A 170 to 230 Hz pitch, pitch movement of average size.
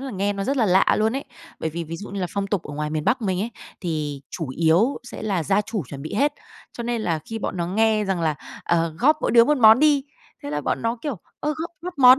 No: high, 205 Hz; wide, 6.4 semitones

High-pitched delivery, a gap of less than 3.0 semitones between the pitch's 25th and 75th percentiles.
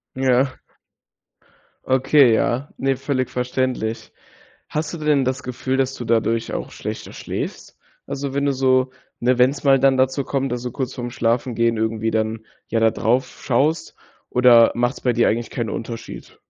No: low, 130 Hz; narrow, 2.4 semitones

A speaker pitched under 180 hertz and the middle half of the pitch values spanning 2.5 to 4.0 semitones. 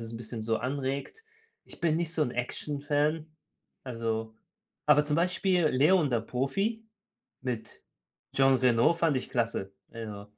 No: low, 135 Hz; average, 5.3 semitones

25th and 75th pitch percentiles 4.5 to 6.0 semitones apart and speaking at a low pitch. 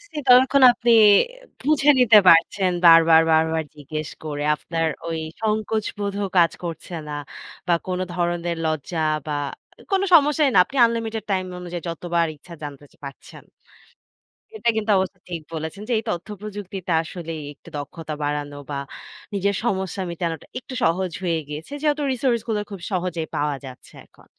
No: average, 5.0 semitones; medium, 175 Hz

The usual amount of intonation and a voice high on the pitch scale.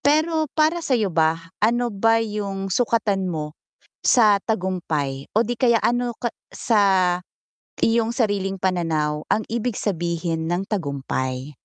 No: wide, 5.9 semitones; high, 200 Hz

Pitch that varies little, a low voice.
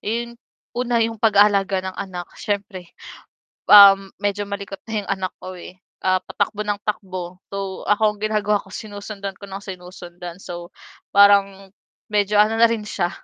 No: narrow, 1.8 semitones; high, 200 Hz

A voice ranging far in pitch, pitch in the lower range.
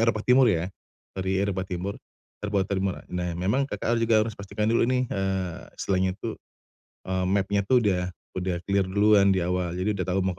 No: narrow, 2.5 semitones; very low, 95 Hz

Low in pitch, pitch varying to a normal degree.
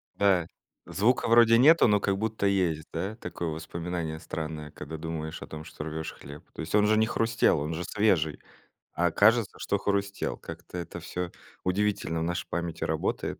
Yes: very low, 90 Hz; average, 4.5 semitones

